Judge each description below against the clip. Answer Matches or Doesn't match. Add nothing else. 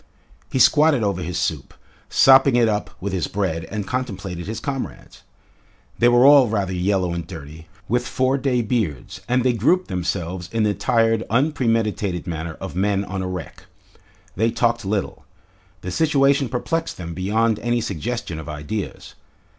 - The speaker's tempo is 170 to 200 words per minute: Doesn't match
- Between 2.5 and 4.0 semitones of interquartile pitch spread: Doesn't match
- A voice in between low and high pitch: Doesn't match